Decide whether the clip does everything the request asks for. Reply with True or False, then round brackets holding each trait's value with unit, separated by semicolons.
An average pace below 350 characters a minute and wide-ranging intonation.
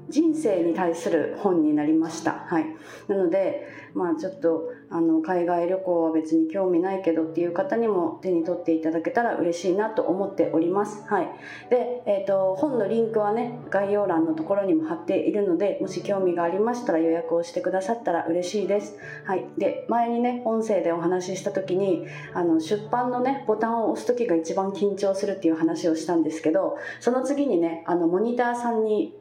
False (365 characters per minute; 5.9 semitones)